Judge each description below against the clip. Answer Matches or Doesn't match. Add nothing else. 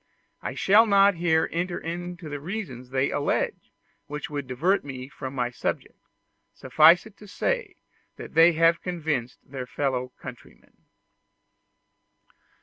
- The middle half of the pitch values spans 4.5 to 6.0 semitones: Matches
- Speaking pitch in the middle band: Matches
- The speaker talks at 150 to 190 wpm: Doesn't match